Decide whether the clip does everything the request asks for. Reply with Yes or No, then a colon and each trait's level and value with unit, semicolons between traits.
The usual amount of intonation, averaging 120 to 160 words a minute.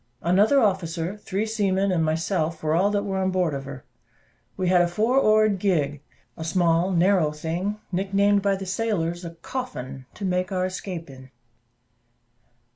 No: average, 3.4 semitones; average, 170 wpm